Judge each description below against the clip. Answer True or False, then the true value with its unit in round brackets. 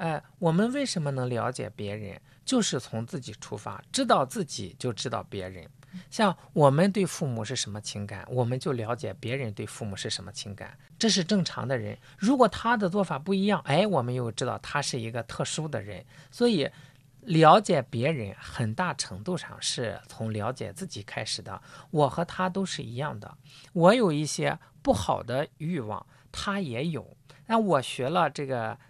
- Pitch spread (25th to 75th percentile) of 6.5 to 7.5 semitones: True (7.1 semitones)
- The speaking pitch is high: False (140 Hz)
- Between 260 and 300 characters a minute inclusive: True (270 characters per minute)